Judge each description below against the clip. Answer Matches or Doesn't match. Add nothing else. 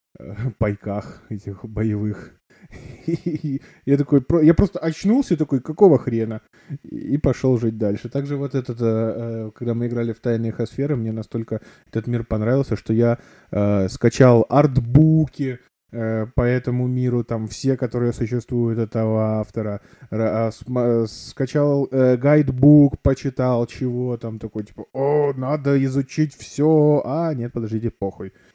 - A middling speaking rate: Matches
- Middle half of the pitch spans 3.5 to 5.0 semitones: Matches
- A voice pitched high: Doesn't match